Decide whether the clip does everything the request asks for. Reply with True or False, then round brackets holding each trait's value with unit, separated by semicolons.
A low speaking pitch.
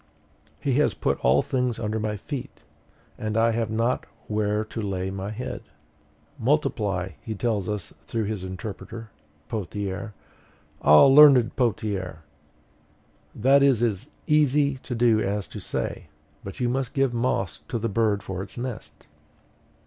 True (110 Hz)